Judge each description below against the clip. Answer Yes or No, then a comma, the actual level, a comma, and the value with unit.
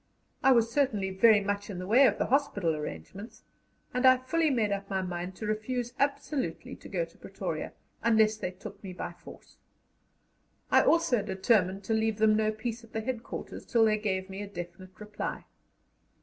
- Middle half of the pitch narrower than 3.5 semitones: No, average, 3.9 semitones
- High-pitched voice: Yes, high, 215 Hz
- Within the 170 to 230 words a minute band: Yes, average, 185 wpm